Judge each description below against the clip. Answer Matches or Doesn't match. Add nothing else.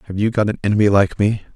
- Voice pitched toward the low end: Matches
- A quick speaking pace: Matches